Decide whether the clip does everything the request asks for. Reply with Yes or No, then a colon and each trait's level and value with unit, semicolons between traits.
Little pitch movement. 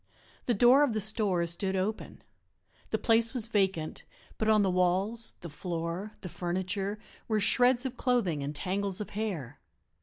No: average, 3.7 semitones